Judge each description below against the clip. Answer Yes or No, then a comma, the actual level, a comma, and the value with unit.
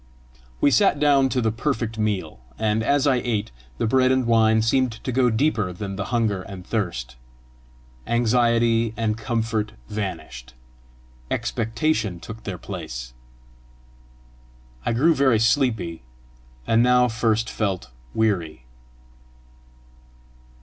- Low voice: Yes, low, 115 Hz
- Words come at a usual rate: No, slow, 120 wpm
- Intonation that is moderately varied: Yes, average, 3.3 semitones